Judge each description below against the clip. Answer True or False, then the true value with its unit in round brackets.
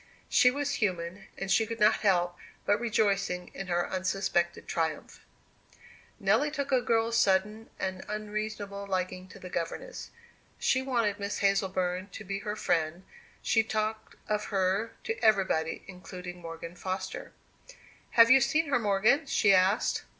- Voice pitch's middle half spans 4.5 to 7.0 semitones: False (3.3 semitones)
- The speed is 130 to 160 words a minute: True (145 wpm)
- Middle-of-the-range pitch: False (200 Hz)